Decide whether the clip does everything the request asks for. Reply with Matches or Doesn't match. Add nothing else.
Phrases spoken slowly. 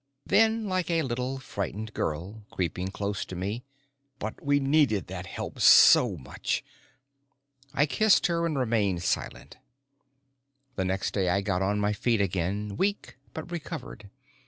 Doesn't match